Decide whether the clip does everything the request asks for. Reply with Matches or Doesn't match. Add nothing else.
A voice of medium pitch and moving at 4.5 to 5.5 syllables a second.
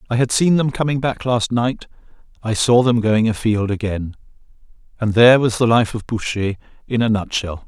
Doesn't match